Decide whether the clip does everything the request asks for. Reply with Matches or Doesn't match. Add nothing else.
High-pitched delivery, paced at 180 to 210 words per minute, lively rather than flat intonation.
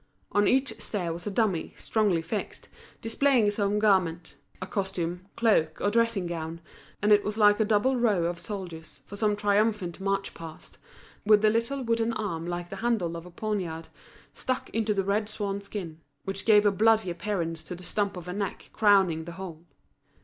Doesn't match